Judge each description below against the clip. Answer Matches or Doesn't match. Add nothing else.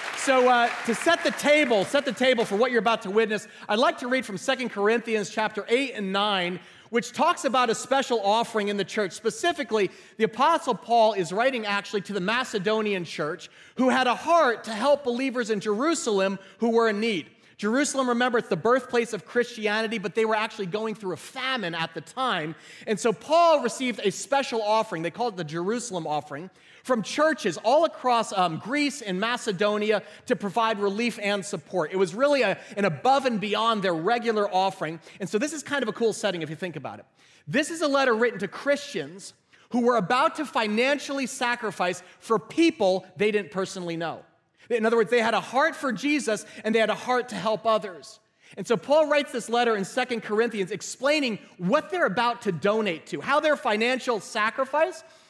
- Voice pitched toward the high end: Matches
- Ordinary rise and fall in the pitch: Matches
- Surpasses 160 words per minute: Matches